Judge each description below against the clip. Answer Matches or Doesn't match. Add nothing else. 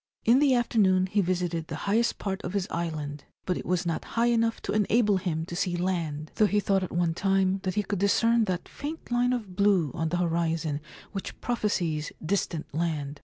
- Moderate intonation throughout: Matches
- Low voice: Doesn't match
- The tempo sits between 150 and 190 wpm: Doesn't match